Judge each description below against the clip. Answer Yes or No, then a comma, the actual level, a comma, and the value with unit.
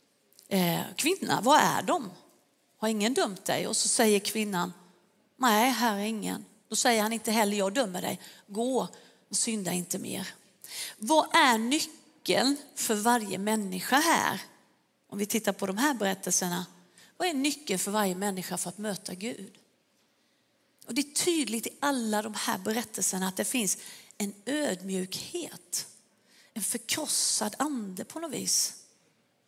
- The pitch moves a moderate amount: Yes, average, 4.7 semitones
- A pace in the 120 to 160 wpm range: Yes, average, 150 wpm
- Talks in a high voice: Yes, high, 220 Hz